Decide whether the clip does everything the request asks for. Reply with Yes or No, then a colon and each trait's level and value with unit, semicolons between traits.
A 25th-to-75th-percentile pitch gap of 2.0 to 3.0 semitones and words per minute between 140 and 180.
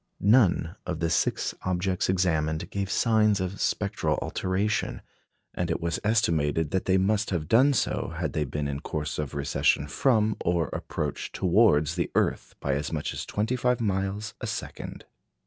No: average, 5.1 semitones; average, 165 wpm